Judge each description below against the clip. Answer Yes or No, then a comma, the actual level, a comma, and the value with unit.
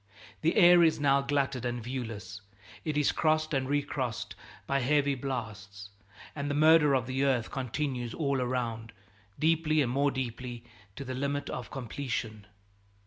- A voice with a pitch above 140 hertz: No, low, 135 Hz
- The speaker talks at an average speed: Yes, average, 150 wpm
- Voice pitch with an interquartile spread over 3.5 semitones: No, average, 3.2 semitones